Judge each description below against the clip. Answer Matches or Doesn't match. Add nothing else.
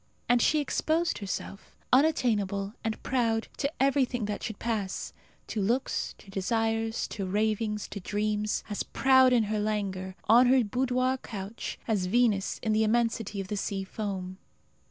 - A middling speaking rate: Matches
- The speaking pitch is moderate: Doesn't match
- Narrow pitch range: Doesn't match